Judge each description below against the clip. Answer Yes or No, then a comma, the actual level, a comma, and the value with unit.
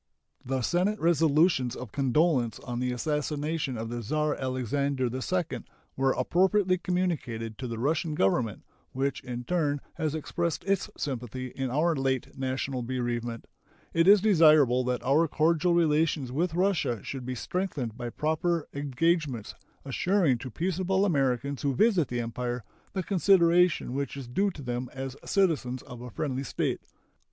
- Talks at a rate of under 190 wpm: Yes, average, 150 wpm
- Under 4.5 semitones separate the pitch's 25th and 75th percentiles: No, average, 5.1 semitones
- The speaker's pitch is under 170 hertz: Yes, medium, 140 Hz